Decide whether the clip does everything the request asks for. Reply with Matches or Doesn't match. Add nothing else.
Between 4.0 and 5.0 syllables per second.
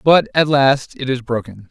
Matches